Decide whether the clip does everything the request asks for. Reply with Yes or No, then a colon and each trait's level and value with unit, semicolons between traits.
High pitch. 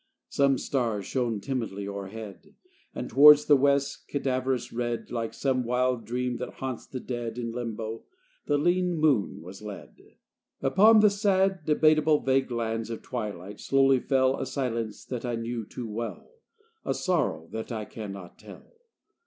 No: low, 125 Hz